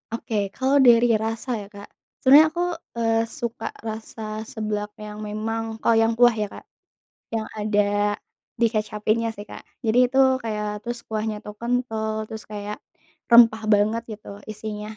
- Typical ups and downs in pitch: No, narrow, 1.7 semitones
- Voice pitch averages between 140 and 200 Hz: No, high, 220 Hz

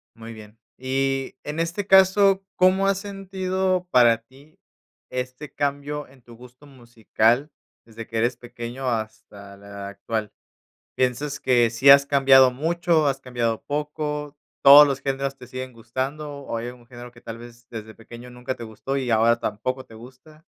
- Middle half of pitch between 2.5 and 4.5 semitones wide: Yes, average, 3.9 semitones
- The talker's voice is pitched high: No, low, 130 Hz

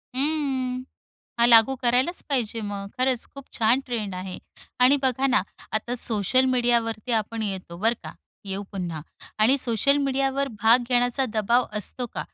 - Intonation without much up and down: No, average, 3.3 semitones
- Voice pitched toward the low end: No, high, 240 Hz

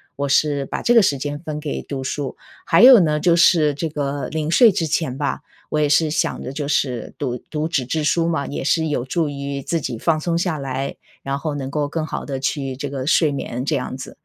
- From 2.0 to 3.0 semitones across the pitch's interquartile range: Yes, average, 2.7 semitones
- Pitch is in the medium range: Yes, medium, 145 Hz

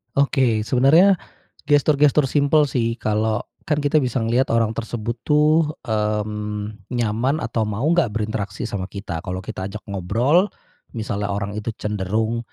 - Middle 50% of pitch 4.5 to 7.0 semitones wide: Yes, average, 4.8 semitones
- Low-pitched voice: Yes, low, 115 Hz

